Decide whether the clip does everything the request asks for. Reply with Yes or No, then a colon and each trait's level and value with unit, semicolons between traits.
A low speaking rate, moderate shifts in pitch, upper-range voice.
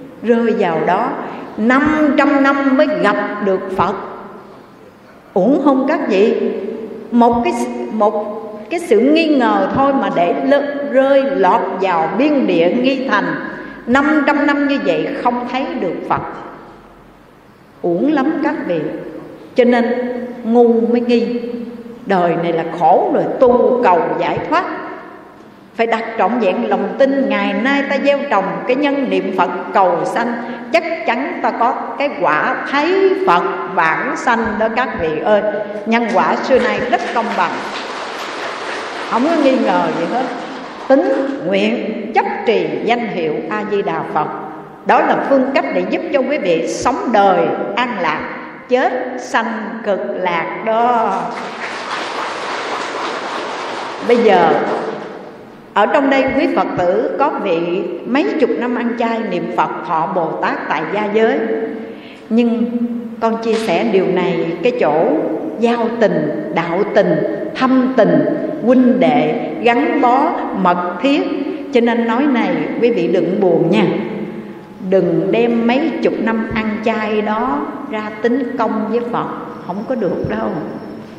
Yes: slow, 150 wpm; average, 4.5 semitones; high, 240 Hz